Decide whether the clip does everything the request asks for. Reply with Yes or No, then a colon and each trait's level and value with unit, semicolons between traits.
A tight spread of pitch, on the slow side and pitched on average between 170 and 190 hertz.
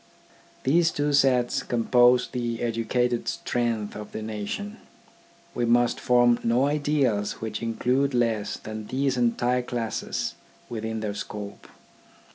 No: narrow, 2.3 semitones; slow, 120 wpm; low, 120 Hz